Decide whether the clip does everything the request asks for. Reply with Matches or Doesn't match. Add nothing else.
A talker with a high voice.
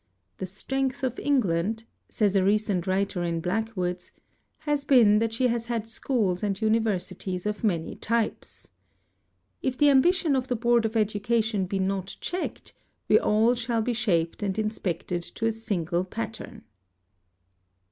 Matches